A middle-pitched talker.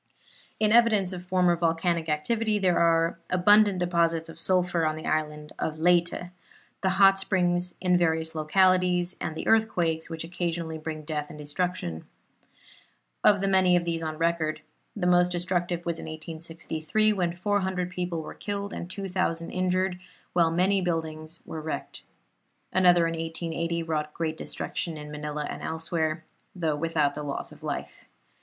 Yes: medium, 170 Hz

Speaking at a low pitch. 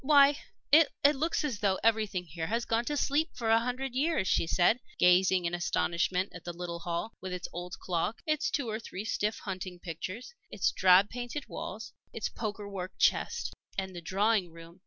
No: high, 200 Hz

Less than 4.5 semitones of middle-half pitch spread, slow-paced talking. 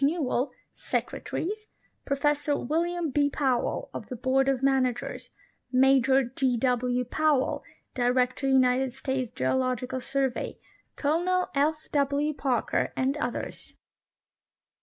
Yes: narrow, 2.5 semitones; slow, 105 wpm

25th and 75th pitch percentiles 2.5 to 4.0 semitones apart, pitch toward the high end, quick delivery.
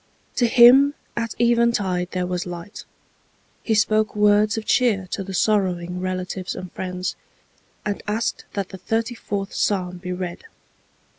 No: average, 3.4 semitones; high, 200 Hz; average, 150 wpm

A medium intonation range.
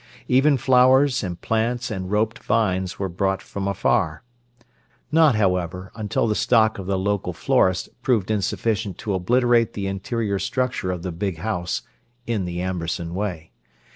Yes: average, 4.2 semitones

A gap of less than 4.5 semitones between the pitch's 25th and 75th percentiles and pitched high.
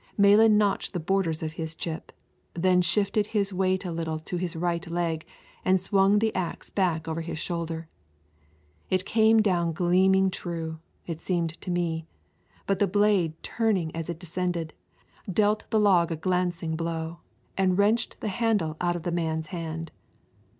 No: average, 3.0 semitones; medium, 175 Hz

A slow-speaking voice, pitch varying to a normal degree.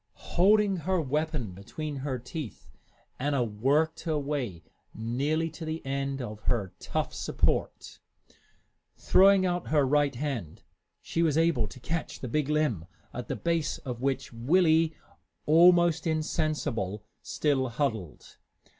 Yes: slow, 130 wpm; average, 4.9 semitones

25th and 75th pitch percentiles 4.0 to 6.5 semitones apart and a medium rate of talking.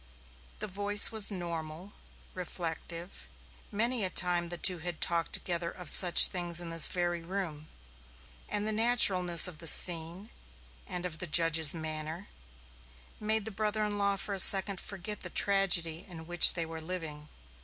No: average, 3.2 semitones; average, 160 wpm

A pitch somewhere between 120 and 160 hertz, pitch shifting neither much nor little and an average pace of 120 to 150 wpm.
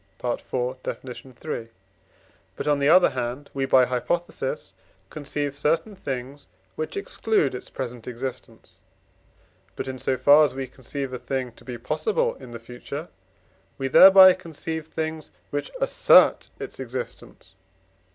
Yes: low, 135 Hz; average, 3.8 semitones; average, 140 wpm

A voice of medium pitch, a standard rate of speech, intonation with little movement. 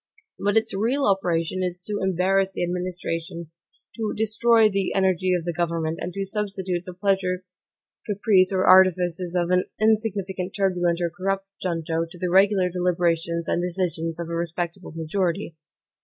Yes: medium, 180 Hz; average, 155 wpm; narrow, 2.2 semitones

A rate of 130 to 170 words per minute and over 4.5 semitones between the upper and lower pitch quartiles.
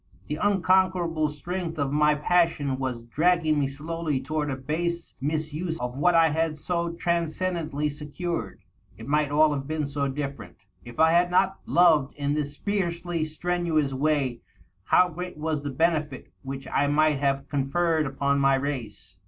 No: average, 160 wpm; average, 3.3 semitones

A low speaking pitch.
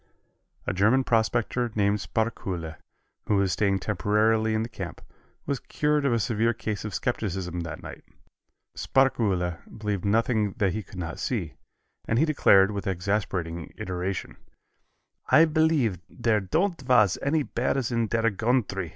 Yes: low, 110 Hz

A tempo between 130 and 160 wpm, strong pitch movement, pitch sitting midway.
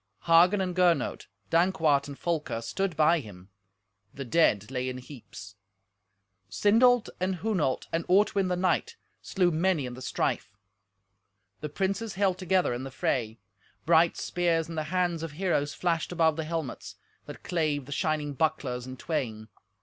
No: average, 155 wpm; average, 4.9 semitones; medium, 165 Hz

